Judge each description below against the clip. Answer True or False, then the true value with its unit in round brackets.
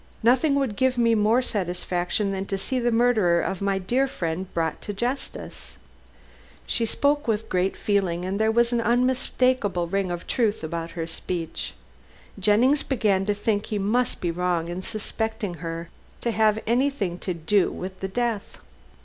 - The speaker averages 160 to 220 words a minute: True (165 wpm)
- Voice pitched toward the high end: True (205 Hz)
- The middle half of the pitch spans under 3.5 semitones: False (4.8 semitones)